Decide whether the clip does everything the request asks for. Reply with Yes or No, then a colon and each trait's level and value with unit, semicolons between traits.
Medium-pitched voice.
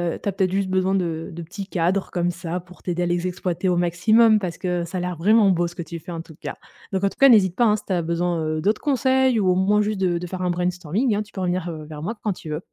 Yes: medium, 180 Hz